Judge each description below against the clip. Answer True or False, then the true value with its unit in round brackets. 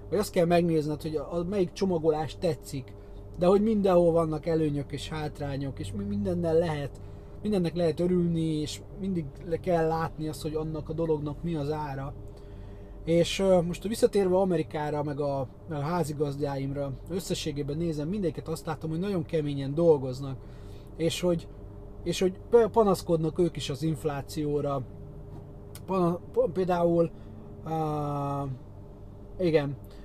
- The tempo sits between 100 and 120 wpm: False (135 wpm)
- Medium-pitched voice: True (155 Hz)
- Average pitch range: True (3.7 semitones)